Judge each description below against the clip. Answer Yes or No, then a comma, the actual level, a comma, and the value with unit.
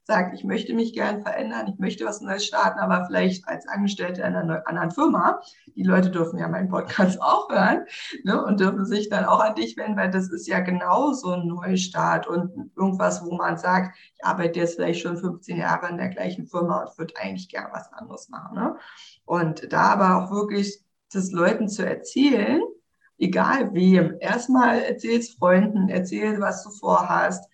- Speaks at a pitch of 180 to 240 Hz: Yes, high, 190 Hz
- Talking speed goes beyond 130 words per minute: Yes, fast, 190 wpm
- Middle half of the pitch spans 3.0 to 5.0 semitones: Yes, average, 3.3 semitones